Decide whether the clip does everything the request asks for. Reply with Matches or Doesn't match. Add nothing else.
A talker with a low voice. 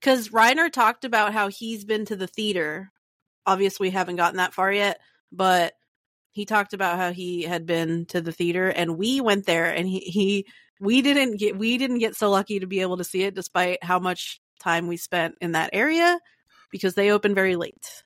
Doesn't match